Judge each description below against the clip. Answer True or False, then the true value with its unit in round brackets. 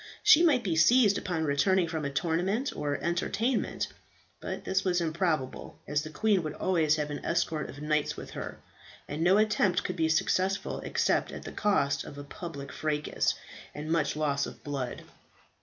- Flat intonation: False (4.3 semitones)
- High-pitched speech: False (160 Hz)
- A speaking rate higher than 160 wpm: True (175 wpm)